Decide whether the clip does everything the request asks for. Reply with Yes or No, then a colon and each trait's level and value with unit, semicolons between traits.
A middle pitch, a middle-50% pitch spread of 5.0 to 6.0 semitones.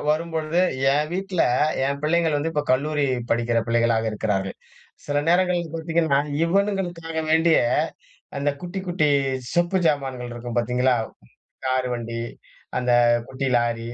Yes: medium, 150 Hz; wide, 5.4 semitones